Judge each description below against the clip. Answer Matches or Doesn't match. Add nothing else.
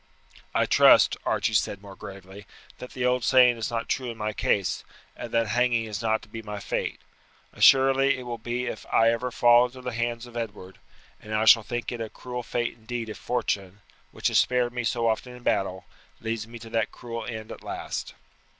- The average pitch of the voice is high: Doesn't match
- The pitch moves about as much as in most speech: Doesn't match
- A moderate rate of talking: Doesn't match